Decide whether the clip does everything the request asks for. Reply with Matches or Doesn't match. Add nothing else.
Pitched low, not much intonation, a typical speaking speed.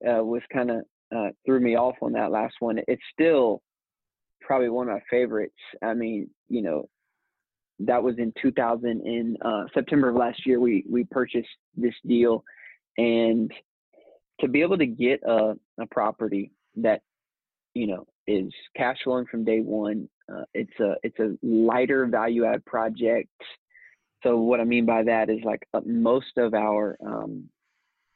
Matches